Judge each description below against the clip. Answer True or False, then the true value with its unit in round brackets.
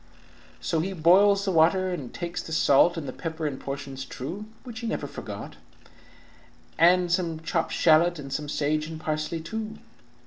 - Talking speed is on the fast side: False (170 wpm)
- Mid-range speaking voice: True (165 Hz)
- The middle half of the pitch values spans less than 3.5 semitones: True (3.1 semitones)